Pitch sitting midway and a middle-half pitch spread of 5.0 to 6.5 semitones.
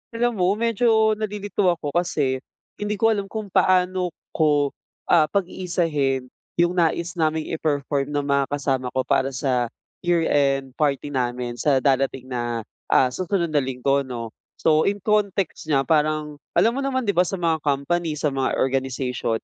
Yes: medium, 155 Hz; wide, 5.4 semitones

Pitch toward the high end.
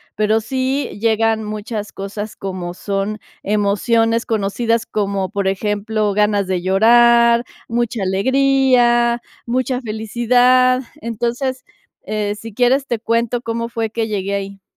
Yes: high, 225 Hz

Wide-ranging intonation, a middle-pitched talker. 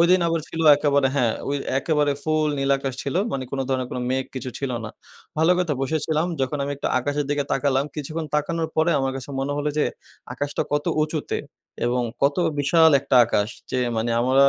No: average, 2.7 semitones; medium, 145 Hz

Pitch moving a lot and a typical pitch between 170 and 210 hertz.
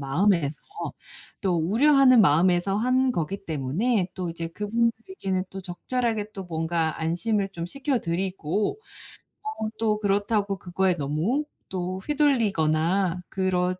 No: average, 4.7 semitones; high, 190 Hz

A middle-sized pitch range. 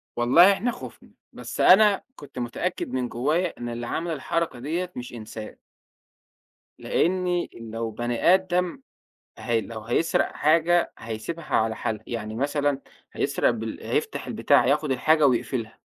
No: wide, 6.4 semitones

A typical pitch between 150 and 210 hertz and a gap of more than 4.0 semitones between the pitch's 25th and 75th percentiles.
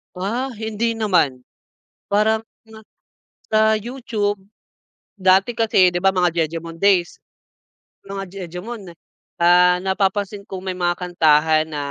No: high, 190 Hz; average, 3.4 semitones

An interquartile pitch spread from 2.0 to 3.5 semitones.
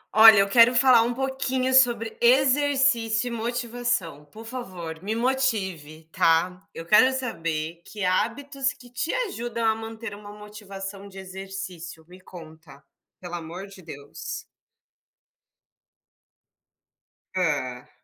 No: wide, 5.6 semitones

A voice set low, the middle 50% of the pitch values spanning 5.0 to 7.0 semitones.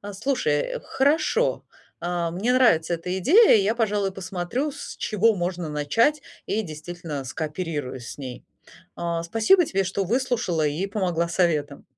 No: medium, 185 Hz; wide, 5.5 semitones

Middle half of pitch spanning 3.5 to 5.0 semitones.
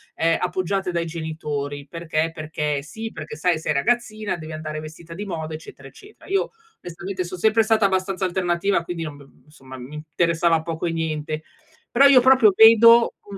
Yes: average, 4.2 semitones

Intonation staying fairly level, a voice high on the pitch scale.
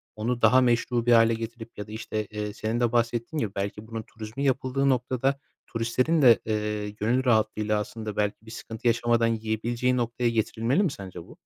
No: narrow, 2.1 semitones; low, 115 Hz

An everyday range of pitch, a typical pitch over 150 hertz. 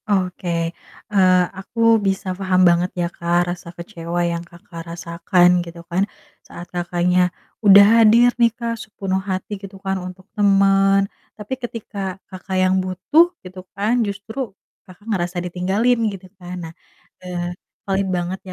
No: narrow, 2.3 semitones; high, 190 Hz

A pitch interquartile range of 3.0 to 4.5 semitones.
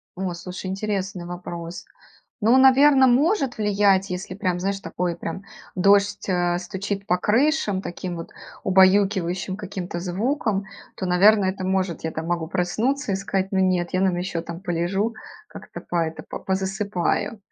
No: narrow, 2.5 semitones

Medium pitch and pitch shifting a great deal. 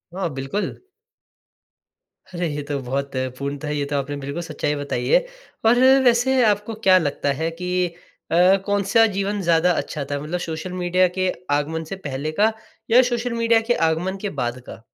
Yes: medium, 175 Hz; wide, 5.9 semitones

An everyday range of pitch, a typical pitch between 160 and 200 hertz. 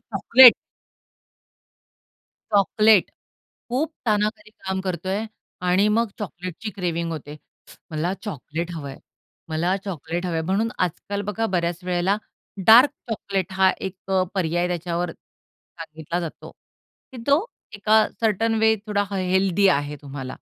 Yes: average, 3.9 semitones; medium, 185 Hz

